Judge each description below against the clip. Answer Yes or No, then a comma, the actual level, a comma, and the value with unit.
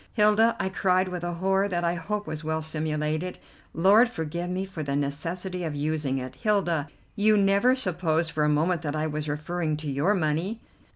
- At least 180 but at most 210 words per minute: Yes, average, 190 wpm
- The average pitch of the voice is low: No, medium, 170 Hz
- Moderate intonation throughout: Yes, average, 3.9 semitones